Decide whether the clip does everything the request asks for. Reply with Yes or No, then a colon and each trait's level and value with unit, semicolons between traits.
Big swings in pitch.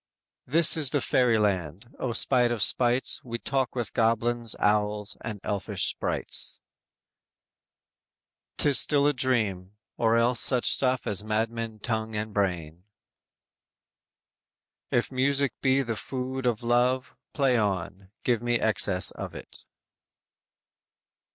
No: average, 3.4 semitones